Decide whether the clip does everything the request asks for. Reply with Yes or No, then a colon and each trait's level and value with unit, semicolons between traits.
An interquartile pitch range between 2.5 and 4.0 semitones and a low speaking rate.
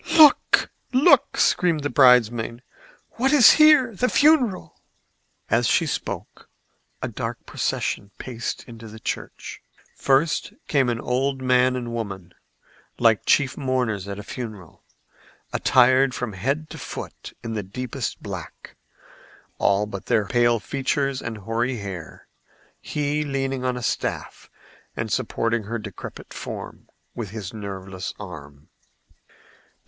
No: average, 4.5 semitones; slow, 130 wpm